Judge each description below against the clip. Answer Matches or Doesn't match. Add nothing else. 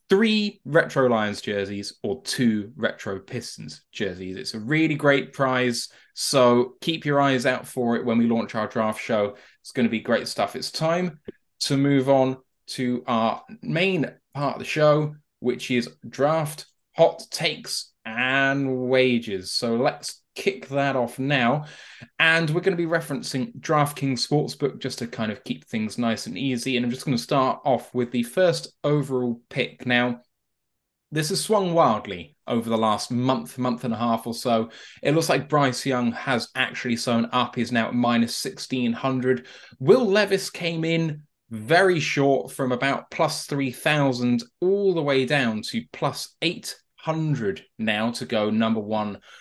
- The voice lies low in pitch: Matches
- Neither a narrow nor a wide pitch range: Matches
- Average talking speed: Matches